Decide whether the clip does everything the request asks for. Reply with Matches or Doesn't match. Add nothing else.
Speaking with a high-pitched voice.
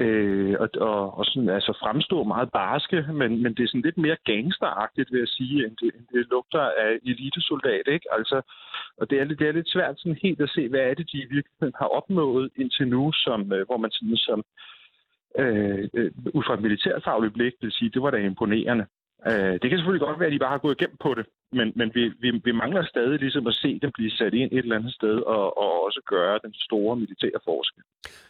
Doesn't match